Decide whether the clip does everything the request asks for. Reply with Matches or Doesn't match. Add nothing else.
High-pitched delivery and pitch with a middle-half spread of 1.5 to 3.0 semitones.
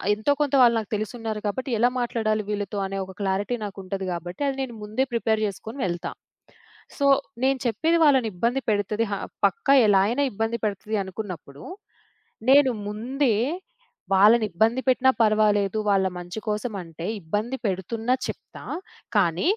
Doesn't match